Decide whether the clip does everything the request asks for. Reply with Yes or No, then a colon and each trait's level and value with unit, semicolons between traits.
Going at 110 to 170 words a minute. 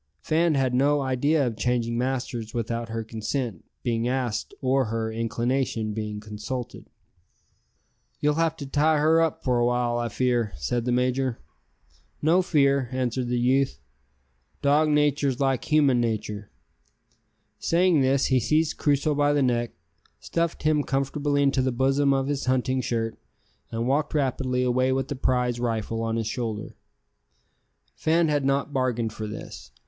Yes: average, 155 wpm